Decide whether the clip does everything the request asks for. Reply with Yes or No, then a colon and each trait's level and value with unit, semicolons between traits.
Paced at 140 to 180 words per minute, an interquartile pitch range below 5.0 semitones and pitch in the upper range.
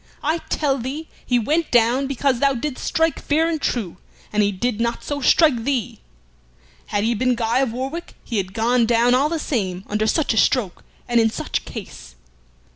No: average, 195 wpm; average, 4.1 semitones; high, 245 Hz